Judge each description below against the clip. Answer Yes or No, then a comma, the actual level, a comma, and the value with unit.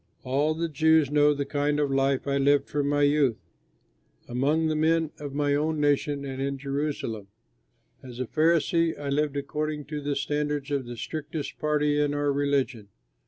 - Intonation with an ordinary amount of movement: No, narrow, 1.5 semitones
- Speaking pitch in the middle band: Yes, medium, 145 Hz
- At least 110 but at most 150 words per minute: No, average, 175 wpm